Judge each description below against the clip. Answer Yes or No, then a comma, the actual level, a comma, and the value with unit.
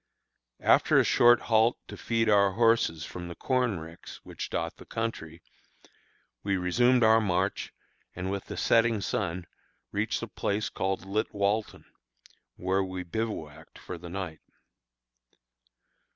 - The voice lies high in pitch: No, low, 100 Hz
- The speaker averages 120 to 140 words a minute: Yes, slow, 135 wpm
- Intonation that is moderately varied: Yes, average, 3.9 semitones